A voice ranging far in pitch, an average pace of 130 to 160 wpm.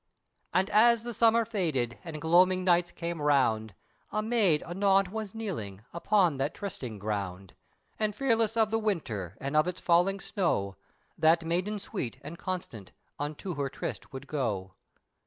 Yes: wide, 7.0 semitones; average, 155 wpm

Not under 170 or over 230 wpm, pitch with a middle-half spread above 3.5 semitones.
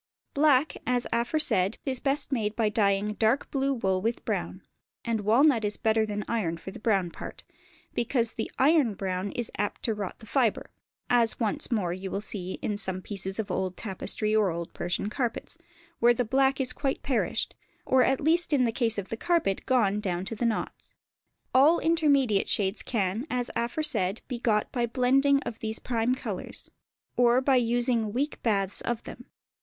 Yes: average, 185 wpm; average, 4.1 semitones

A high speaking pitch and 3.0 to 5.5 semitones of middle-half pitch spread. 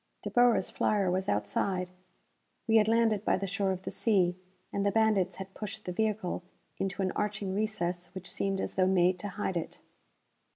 No: high, 195 Hz; narrow, 2.6 semitones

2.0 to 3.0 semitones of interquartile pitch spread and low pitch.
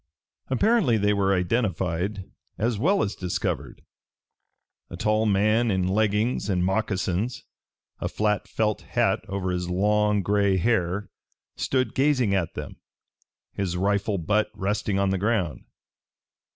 Yes: narrow, 2.5 semitones; low, 100 Hz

